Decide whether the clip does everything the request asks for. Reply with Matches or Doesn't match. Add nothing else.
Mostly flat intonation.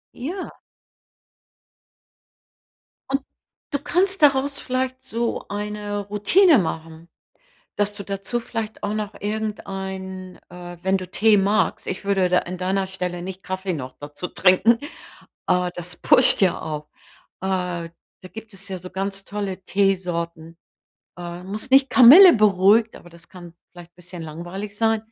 Doesn't match